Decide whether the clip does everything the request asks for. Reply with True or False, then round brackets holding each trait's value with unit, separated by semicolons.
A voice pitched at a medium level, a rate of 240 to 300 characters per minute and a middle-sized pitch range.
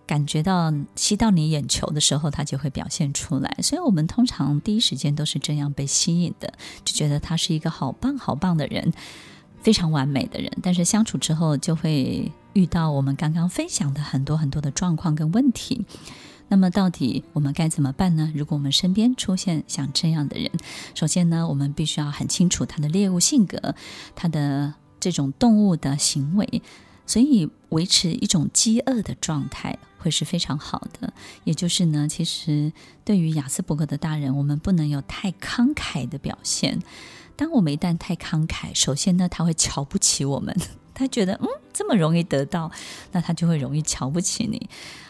True (165 Hz; 285 characters per minute; 4.6 semitones)